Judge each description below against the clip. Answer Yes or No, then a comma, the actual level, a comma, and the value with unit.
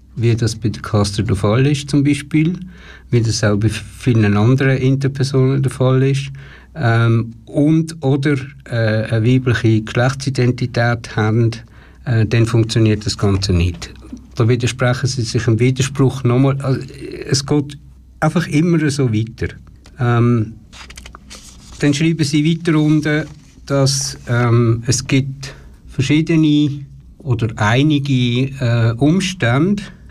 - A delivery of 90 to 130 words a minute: Yes, slow, 125 wpm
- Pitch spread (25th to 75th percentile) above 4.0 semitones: No, average, 3.7 semitones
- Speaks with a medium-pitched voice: No, low, 125 Hz